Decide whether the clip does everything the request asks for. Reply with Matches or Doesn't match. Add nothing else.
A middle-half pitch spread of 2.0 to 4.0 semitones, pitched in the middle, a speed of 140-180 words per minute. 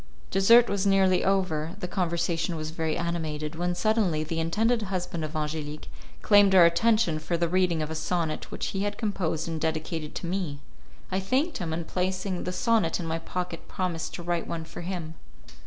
Doesn't match